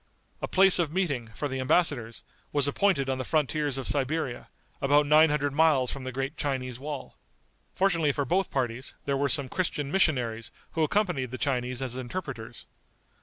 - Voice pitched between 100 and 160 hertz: Yes, medium, 140 Hz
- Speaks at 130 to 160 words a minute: No, average, 170 wpm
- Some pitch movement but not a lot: Yes, average, 3.2 semitones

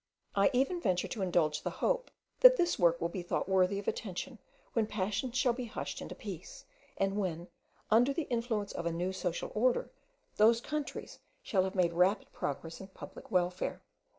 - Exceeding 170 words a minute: Yes, average, 180 wpm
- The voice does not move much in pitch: No, average, 5.0 semitones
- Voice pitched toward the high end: Yes, high, 195 Hz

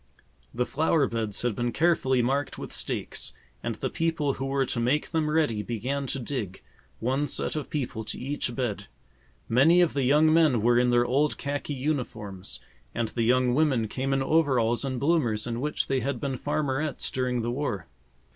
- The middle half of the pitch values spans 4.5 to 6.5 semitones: No, average, 3.6 semitones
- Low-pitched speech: Yes, low, 130 Hz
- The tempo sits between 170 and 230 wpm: Yes, average, 185 wpm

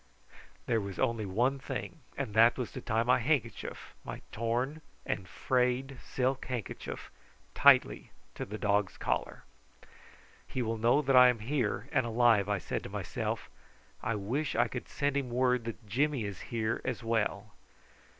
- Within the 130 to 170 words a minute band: Yes, average, 160 wpm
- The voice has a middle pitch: No, low, 120 Hz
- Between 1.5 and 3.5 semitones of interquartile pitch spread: Yes, average, 3.1 semitones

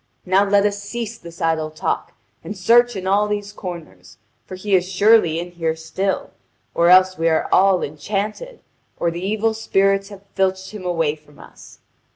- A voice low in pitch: No, high, 190 Hz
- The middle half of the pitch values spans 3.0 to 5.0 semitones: Yes, average, 3.4 semitones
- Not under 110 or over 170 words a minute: No, average, 180 wpm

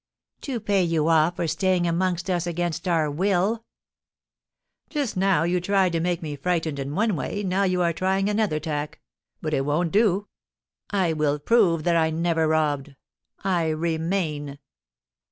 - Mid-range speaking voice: Yes, medium, 175 Hz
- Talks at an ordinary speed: Yes, average, 160 wpm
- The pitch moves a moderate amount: Yes, average, 3.3 semitones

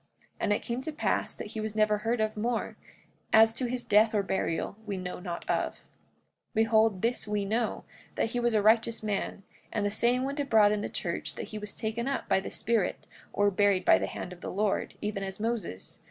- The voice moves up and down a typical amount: No, narrow, 2.2 semitones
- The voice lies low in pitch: No, high, 215 Hz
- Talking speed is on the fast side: Yes, fast, 225 wpm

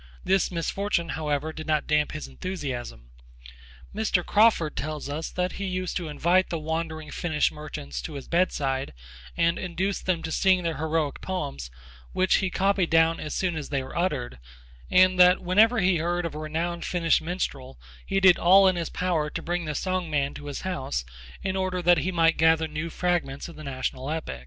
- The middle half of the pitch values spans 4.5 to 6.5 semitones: No, average, 3.3 semitones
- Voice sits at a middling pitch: Yes, medium, 165 Hz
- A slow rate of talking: No, average, 190 wpm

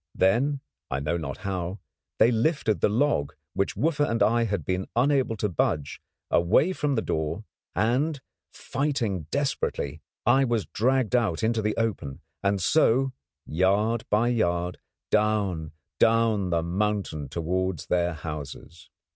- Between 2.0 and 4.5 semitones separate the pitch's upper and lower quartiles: No, wide, 5.6 semitones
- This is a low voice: Yes, low, 105 Hz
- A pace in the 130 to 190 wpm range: Yes, average, 140 wpm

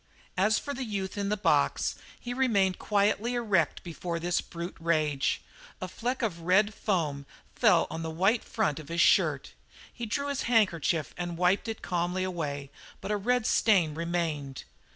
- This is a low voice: No, medium, 185 Hz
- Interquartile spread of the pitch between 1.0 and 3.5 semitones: No, average, 4.5 semitones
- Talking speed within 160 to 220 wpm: Yes, average, 170 wpm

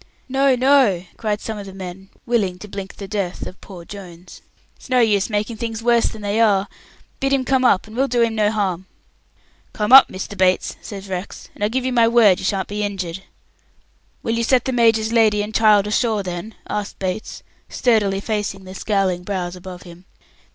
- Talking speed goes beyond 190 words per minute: Yes, average, 200 wpm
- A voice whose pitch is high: Yes, high, 210 Hz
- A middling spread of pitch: Yes, average, 3.2 semitones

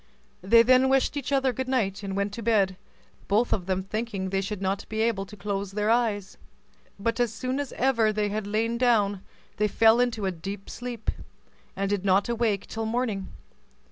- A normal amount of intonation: Yes, average, 3.1 semitones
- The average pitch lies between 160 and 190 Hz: No, high, 215 Hz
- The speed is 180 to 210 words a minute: Yes, average, 195 wpm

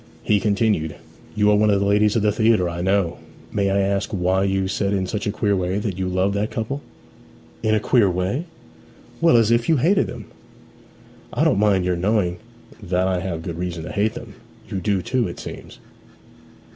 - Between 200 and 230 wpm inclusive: Yes, fast, 205 wpm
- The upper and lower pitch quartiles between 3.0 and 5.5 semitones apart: No, narrow, 2.5 semitones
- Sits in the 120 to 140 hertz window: No, low, 100 Hz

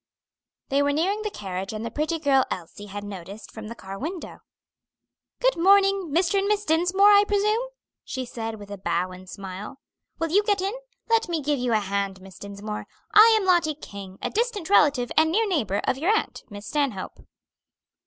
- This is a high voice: Yes, very high, 285 Hz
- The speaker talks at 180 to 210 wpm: Yes, average, 195 wpm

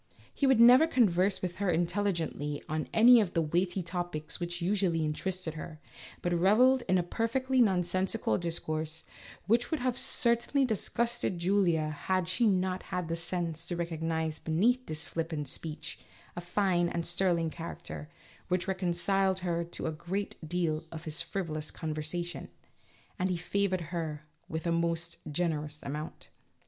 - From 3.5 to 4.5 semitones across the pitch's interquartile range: No, average, 3.1 semitones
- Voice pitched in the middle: Yes, medium, 175 Hz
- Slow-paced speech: No, average, 155 wpm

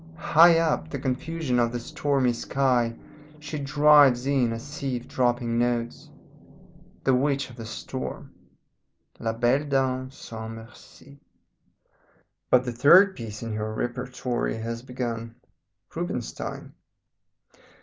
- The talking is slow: Yes, slow, 120 wpm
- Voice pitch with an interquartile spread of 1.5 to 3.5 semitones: Yes, average, 3.1 semitones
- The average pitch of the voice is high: No, low, 125 Hz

